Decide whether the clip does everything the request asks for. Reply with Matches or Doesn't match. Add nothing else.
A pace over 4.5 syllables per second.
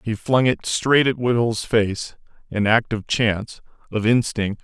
Doesn't match